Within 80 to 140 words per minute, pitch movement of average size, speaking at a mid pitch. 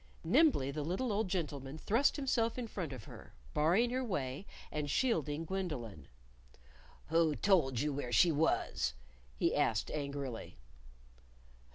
No: slow, 135 wpm; wide, 6.5 semitones; medium, 160 Hz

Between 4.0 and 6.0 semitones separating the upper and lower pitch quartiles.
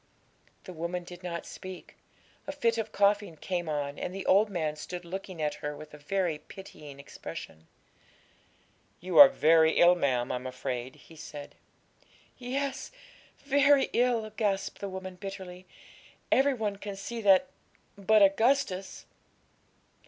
Yes: average, 5.2 semitones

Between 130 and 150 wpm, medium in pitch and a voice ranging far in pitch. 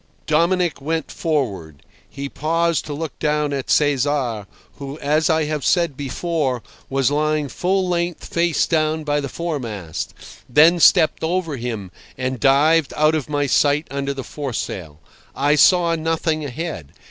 No: average, 145 wpm; medium, 150 Hz; average, 3.0 semitones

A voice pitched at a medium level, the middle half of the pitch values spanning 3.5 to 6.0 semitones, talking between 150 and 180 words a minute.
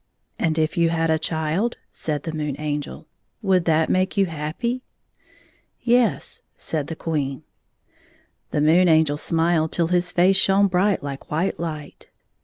No: medium, 165 Hz; average, 3.1 semitones; average, 160 wpm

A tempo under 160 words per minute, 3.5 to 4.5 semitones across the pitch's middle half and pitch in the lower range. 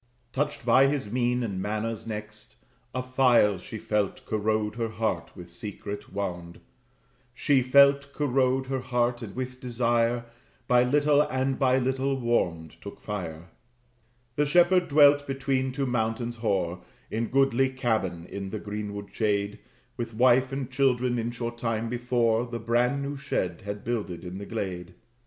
Yes: average, 150 wpm; average, 3.9 semitones; low, 120 Hz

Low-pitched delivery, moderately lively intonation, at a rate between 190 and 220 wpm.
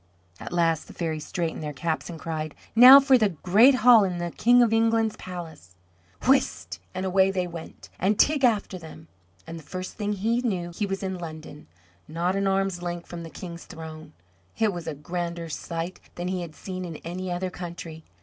No: medium, 175 Hz; average, 3.1 semitones; average, 200 wpm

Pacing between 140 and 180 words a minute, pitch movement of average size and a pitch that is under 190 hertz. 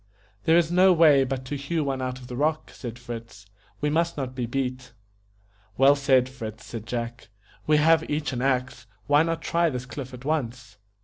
No: average, 195 wpm; average, 3.4 semitones; low, 135 Hz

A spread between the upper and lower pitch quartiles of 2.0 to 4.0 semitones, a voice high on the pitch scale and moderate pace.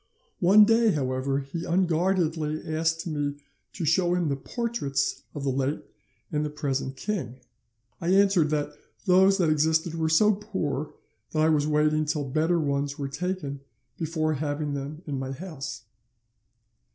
No: average, 3.6 semitones; medium, 155 Hz; average, 150 wpm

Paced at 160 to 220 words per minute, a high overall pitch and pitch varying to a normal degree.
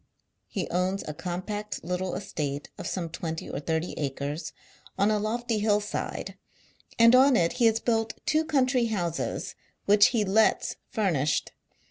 No: average, 150 wpm; high, 200 Hz; average, 5.0 semitones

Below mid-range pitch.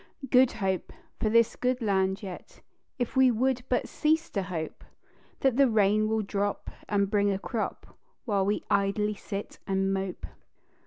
No: high, 210 Hz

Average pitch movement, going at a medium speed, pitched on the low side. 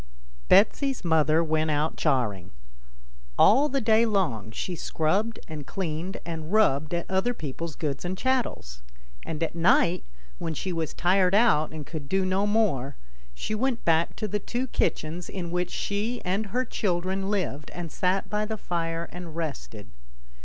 No: average, 4.8 semitones; average, 160 wpm; medium, 175 Hz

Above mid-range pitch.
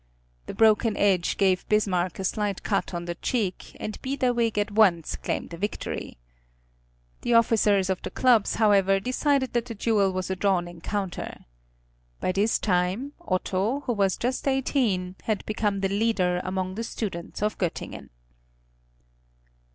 Yes: high, 205 Hz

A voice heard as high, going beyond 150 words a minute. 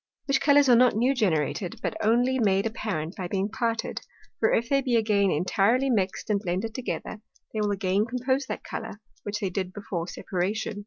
Yes: high, 215 Hz; average, 190 wpm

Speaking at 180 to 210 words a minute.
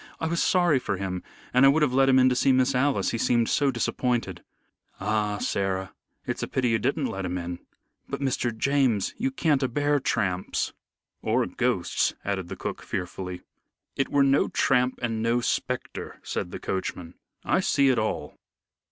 Yes: average, 185 wpm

